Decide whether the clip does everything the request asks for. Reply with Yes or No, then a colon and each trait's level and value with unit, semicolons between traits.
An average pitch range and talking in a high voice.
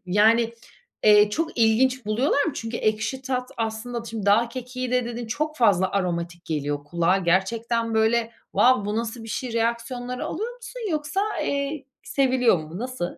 Yes: average, 3.5 semitones; high, 230 Hz